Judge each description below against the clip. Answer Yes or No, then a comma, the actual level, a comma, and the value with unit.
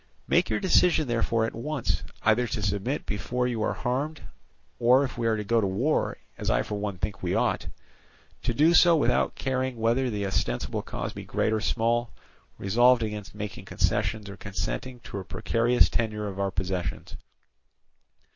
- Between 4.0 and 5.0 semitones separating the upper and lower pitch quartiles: No, average, 3.4 semitones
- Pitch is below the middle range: Yes, low, 115 Hz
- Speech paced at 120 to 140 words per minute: No, average, 175 wpm